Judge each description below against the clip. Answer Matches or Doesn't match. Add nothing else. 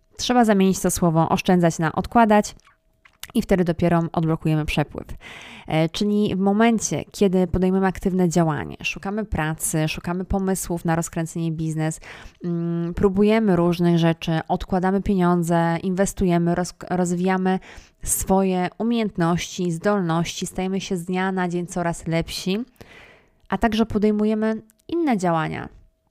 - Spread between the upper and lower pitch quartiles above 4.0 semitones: Doesn't match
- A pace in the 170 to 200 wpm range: Doesn't match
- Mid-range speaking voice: Matches